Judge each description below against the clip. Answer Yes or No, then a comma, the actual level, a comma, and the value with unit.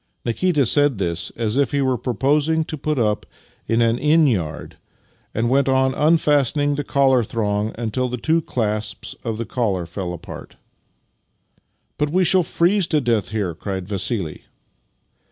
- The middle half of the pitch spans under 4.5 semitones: No, wide, 5.6 semitones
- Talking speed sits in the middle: Yes, average, 165 wpm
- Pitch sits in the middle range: No, low, 125 Hz